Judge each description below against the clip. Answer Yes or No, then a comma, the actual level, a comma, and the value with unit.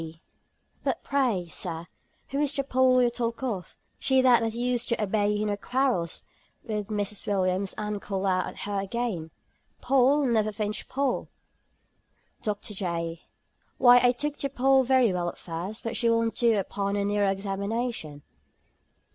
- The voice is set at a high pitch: Yes, high, 215 Hz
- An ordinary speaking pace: Yes, average, 165 wpm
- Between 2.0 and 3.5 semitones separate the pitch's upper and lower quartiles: No, average, 4.1 semitones